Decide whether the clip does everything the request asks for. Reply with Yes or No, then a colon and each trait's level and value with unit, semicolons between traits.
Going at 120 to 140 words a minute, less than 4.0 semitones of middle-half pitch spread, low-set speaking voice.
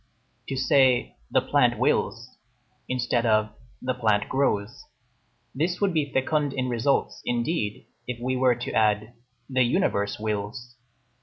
Yes: slow, 135 wpm; average, 3.6 semitones; low, 125 Hz